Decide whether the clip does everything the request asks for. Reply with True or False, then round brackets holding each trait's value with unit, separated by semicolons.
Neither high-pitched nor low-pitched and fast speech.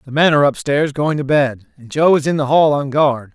True (145 Hz; 270 wpm)